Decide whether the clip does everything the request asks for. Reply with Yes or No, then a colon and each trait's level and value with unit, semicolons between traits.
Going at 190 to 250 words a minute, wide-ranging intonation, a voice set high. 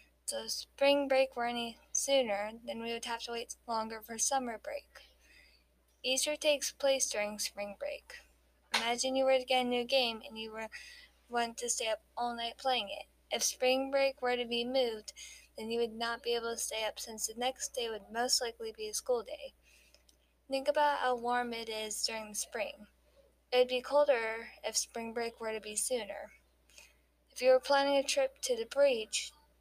No: average, 200 wpm; average, 3.4 semitones; high, 240 Hz